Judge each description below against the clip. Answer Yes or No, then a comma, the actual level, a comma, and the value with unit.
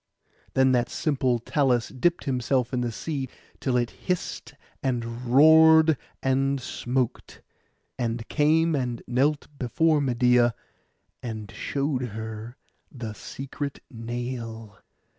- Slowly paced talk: Yes, slow, 110 wpm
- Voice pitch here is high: No, low, 125 Hz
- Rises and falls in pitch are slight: No, average, 3.0 semitones